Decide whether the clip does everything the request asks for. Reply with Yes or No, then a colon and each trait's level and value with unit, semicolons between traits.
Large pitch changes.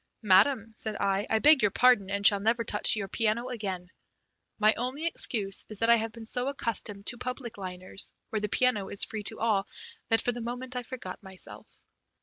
No: average, 3.4 semitones